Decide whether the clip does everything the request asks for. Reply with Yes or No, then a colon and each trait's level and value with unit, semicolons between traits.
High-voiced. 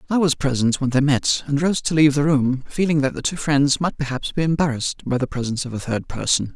No: medium, 140 Hz